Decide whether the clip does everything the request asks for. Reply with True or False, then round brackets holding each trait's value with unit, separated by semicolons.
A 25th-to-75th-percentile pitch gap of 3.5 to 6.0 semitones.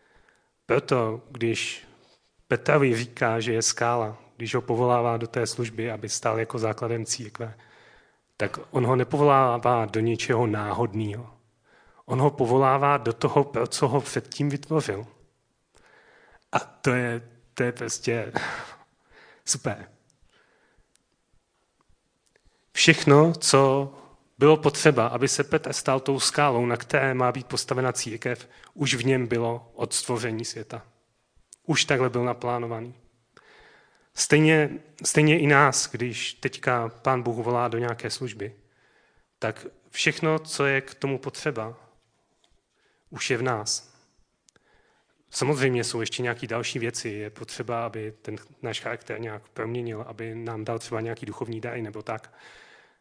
False (2.8 semitones)